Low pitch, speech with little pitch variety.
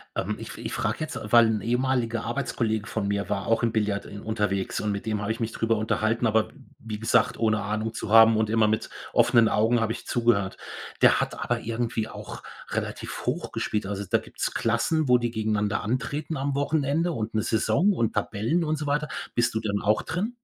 Yes: low, 115 Hz; narrow, 2.2 semitones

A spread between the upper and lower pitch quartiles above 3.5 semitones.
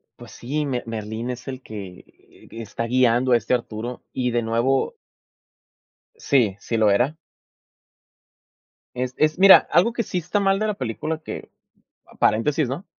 Yes: average, 5.1 semitones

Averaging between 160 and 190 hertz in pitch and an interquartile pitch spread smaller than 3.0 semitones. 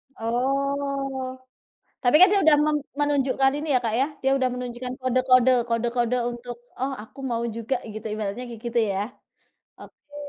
No: very high, 255 Hz; narrow, 2.5 semitones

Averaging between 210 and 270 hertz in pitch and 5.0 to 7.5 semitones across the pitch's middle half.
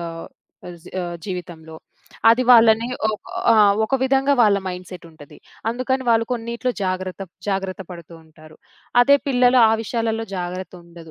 No: high, 195 Hz; average, 5.3 semitones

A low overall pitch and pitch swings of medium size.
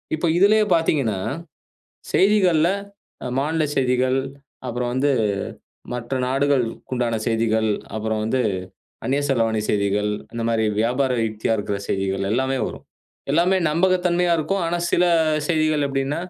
No: low, 130 Hz; wide, 6.2 semitones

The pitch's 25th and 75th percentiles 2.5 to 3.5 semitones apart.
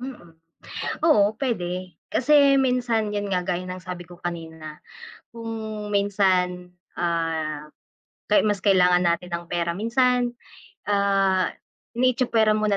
No: average, 4.2 semitones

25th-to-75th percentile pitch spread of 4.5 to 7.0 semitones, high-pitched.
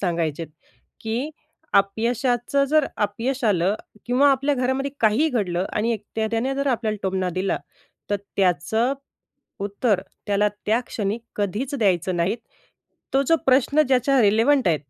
Yes: average, 5.0 semitones; high, 225 Hz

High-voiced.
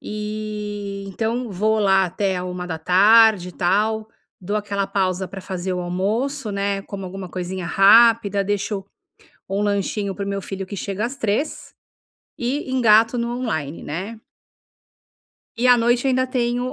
Yes: high, 205 Hz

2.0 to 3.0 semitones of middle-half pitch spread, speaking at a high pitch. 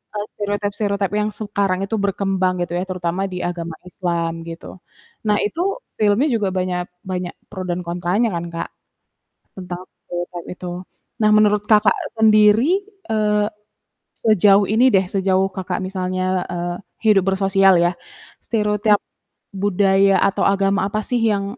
Yes: narrow, 2.5 semitones; high, 195 Hz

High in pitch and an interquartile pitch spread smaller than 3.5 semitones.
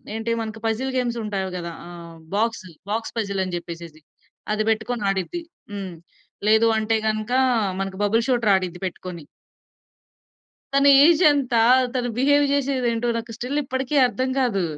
No: high, 225 Hz; average, 4.8 semitones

